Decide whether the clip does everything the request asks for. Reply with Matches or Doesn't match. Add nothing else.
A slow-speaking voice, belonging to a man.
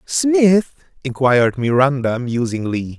Matches